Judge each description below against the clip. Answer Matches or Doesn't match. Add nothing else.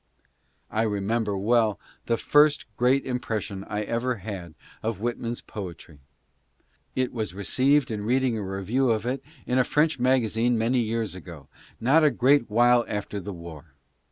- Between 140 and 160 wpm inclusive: Matches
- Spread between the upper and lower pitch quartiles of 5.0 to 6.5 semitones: Doesn't match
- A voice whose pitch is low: Matches